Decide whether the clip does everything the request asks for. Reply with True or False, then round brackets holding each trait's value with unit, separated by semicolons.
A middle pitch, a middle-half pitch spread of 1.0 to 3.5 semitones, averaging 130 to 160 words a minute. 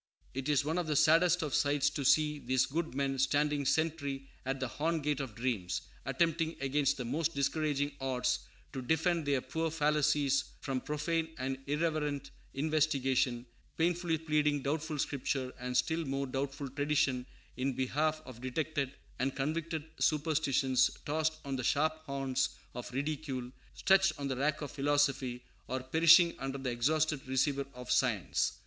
True (145 Hz; 2.8 semitones; 155 wpm)